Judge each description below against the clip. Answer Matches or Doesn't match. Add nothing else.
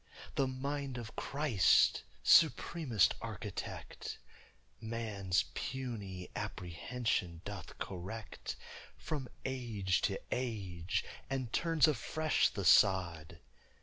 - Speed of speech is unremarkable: Doesn't match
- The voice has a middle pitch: Doesn't match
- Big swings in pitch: Matches